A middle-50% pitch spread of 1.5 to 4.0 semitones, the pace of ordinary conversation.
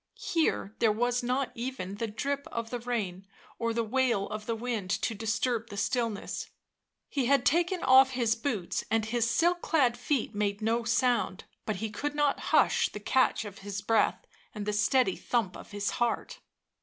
Yes: average, 3.5 semitones; average, 180 wpm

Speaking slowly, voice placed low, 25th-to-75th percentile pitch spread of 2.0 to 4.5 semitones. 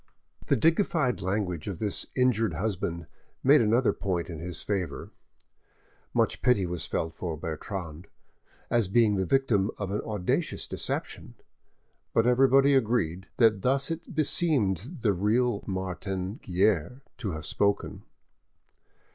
No: slow, 130 wpm; low, 105 Hz; wide, 5.4 semitones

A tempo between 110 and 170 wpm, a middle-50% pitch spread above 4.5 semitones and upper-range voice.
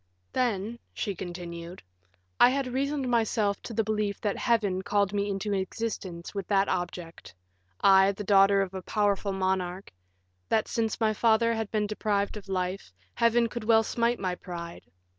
No: average, 160 wpm; average, 2.8 semitones; high, 200 Hz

